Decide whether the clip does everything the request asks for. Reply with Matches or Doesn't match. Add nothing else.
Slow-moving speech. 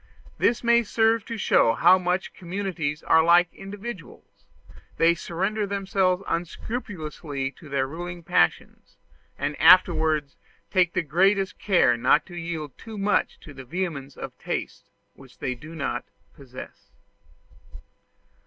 Matches